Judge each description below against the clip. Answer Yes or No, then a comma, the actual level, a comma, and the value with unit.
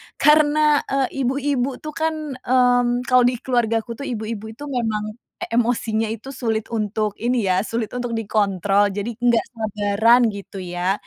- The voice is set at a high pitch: Yes, high, 235 Hz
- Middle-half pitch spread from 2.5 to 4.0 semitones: Yes, average, 3.0 semitones